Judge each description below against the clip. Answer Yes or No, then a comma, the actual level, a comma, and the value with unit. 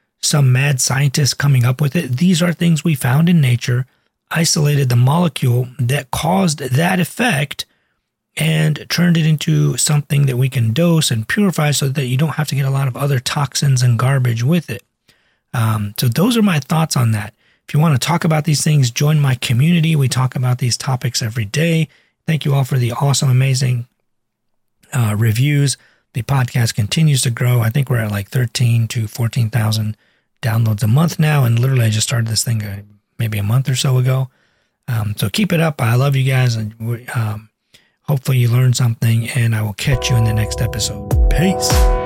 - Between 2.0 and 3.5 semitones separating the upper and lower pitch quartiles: No, average, 4.0 semitones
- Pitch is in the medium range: No, low, 130 Hz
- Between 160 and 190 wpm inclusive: No, average, 200 wpm